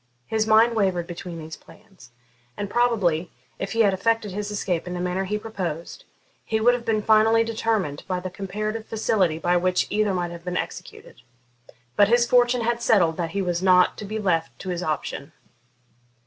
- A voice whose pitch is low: No, high, 195 Hz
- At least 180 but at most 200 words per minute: Yes, average, 190 wpm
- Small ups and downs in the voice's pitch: No, average, 3.8 semitones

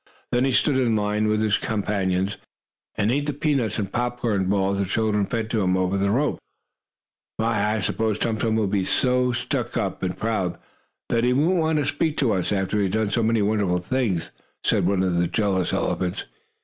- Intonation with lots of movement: No, average, 3.7 semitones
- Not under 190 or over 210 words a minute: Yes, fast, 205 wpm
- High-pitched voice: No, low, 105 Hz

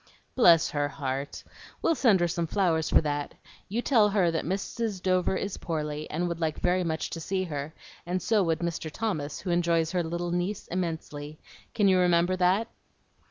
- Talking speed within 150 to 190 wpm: Yes, average, 185 wpm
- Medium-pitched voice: Yes, medium, 175 Hz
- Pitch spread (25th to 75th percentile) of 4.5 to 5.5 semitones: No, average, 2.8 semitones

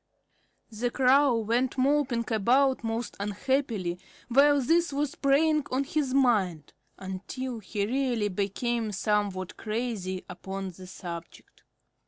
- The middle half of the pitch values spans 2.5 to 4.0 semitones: No, average, 5.3 semitones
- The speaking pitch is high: Yes, high, 235 Hz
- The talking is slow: Yes, slow, 115 wpm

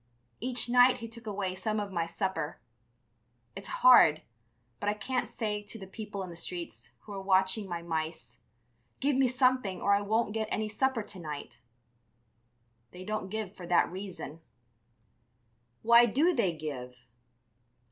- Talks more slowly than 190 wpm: Yes, average, 155 wpm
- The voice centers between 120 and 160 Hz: No, high, 200 Hz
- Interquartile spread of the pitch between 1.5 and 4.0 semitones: No, average, 4.6 semitones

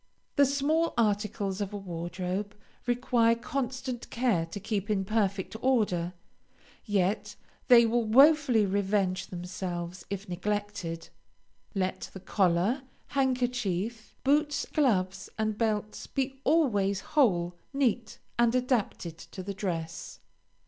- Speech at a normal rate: No, slow, 115 wpm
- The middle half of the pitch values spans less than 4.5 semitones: No, average, 4.8 semitones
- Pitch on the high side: Yes, high, 210 Hz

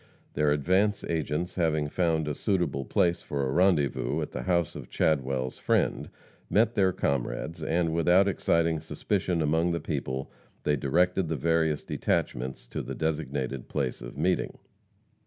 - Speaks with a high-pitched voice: No, very low, 80 Hz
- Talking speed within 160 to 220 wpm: No, average, 150 wpm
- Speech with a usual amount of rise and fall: Yes, average, 3.8 semitones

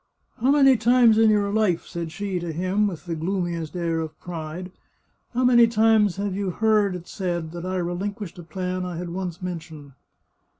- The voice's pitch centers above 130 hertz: Yes, medium, 185 Hz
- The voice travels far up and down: No, average, 3.6 semitones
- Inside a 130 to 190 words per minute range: No, average, 200 wpm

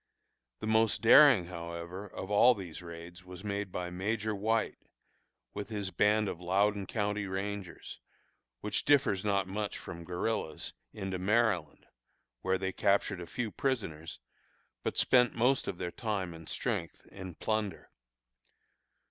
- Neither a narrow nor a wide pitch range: Yes, average, 3.2 semitones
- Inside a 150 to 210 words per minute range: No, average, 140 wpm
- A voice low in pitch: Yes, low, 100 Hz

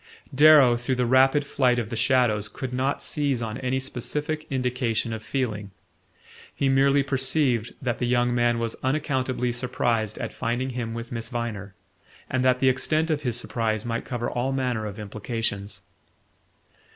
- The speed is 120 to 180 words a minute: Yes, average, 165 wpm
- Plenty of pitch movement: No, narrow, 2.4 semitones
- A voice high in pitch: No, low, 125 Hz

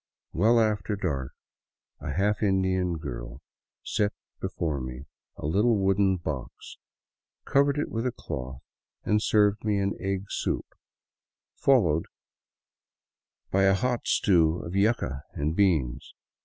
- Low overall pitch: Yes, very low, 95 Hz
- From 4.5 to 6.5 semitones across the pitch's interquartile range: Yes, wide, 5.5 semitones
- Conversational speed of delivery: No, slow, 125 wpm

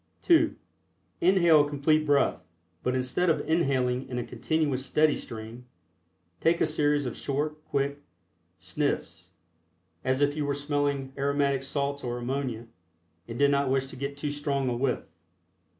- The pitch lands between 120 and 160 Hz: Yes, medium, 140 Hz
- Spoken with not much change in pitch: Yes, narrow, 2.1 semitones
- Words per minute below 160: Yes, average, 150 wpm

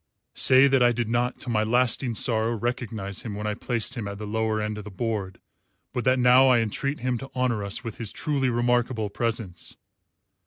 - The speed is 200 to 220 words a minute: Yes, fast, 205 wpm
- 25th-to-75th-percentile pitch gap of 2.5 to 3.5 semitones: Yes, average, 2.8 semitones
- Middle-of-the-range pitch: No, low, 115 Hz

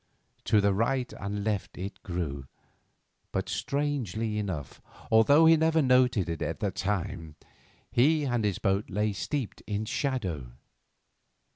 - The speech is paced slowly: Yes, slow, 130 wpm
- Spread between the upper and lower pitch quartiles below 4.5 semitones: No, wide, 5.5 semitones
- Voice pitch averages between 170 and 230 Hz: No, low, 105 Hz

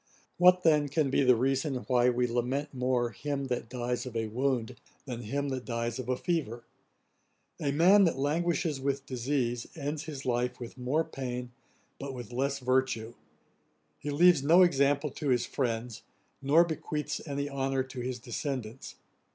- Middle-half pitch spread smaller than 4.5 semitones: Yes, average, 2.8 semitones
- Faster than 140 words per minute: Yes, average, 165 wpm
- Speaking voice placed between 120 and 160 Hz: Yes, low, 135 Hz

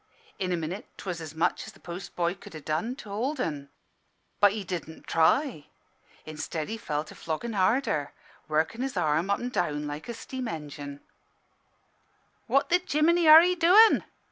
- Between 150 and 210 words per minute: Yes, average, 175 wpm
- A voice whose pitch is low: No, medium, 180 Hz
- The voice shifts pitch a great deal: Yes, wide, 8.3 semitones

